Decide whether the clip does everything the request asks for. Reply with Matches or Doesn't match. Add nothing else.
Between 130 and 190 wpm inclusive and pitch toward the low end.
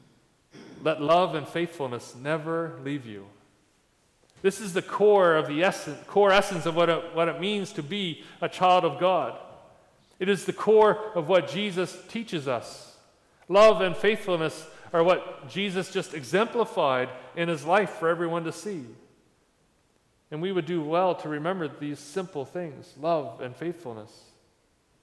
Doesn't match